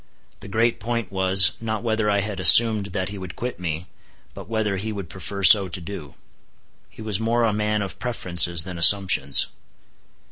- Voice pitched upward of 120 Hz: No, low, 100 Hz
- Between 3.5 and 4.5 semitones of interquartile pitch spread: No, average, 3.0 semitones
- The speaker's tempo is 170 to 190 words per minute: Yes, average, 180 wpm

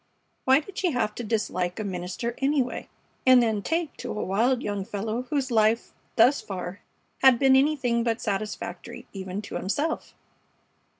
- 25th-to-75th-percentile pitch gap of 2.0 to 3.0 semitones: No, average, 4.6 semitones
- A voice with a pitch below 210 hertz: No, high, 230 Hz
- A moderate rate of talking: Yes, average, 160 wpm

